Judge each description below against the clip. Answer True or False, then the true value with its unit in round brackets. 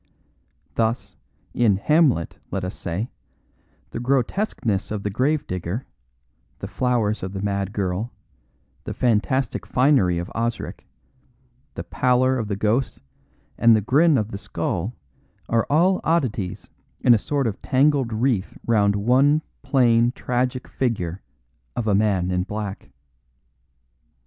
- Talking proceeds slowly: True (130 wpm)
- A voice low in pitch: True (115 Hz)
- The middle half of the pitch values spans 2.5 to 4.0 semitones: False (4.4 semitones)